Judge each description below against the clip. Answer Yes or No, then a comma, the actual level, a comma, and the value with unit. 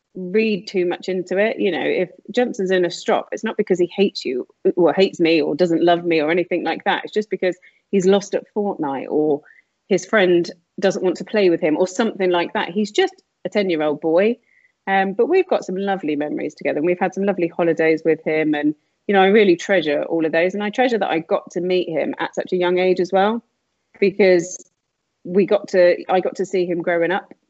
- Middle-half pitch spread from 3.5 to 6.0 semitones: No, average, 2.8 semitones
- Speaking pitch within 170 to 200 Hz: Yes, medium, 185 Hz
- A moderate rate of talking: No, fast, 235 wpm